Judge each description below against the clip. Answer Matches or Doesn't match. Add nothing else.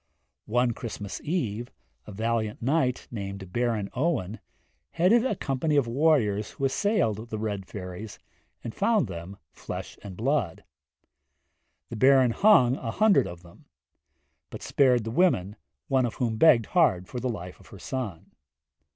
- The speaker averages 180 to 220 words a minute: Doesn't match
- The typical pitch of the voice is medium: Doesn't match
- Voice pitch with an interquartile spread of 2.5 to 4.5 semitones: Doesn't match